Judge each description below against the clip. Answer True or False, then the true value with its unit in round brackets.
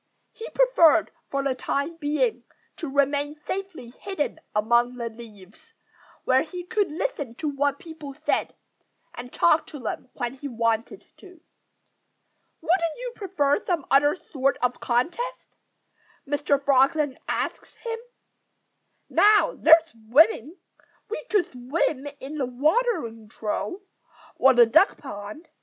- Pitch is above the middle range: True (290 Hz)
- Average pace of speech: False (130 wpm)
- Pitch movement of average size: False (5.7 semitones)